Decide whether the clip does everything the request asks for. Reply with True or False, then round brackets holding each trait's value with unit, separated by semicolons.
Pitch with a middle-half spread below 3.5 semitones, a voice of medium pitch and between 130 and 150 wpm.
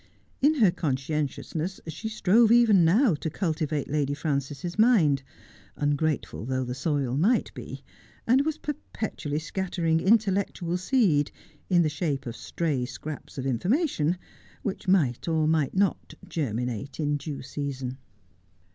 False (5.2 semitones; 160 Hz; 140 wpm)